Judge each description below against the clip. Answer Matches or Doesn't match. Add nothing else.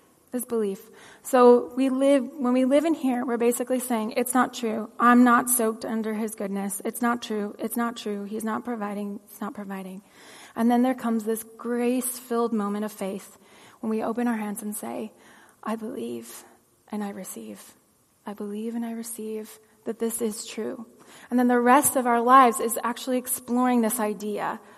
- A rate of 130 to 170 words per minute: Doesn't match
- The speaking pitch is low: Doesn't match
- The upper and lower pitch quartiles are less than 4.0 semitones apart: Matches